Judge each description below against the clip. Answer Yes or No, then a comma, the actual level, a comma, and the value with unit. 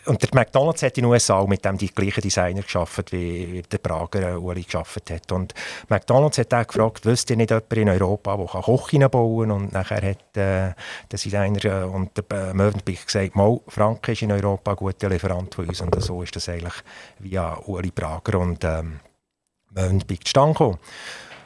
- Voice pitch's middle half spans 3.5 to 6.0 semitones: No, average, 3.1 semitones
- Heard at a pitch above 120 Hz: No, low, 100 Hz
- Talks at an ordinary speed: No, fast, 195 wpm